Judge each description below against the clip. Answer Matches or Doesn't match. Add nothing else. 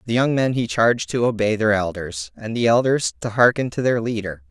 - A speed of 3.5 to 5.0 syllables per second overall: Doesn't match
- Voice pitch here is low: Matches